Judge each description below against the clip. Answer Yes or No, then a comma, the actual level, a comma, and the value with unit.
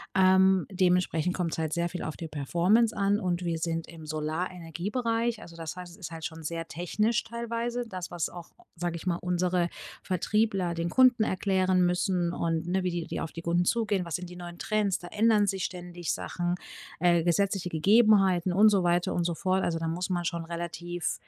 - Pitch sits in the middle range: Yes, medium, 180 Hz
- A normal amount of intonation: No, narrow, 2.3 semitones